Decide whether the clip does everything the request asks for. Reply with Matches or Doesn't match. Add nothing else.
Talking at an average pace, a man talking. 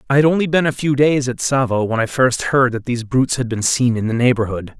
Doesn't match